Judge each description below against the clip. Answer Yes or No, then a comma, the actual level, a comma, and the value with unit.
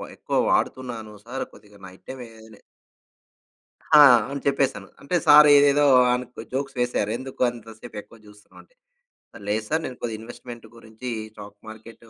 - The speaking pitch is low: Yes, low, 120 Hz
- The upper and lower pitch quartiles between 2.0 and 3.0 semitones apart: No, average, 3.4 semitones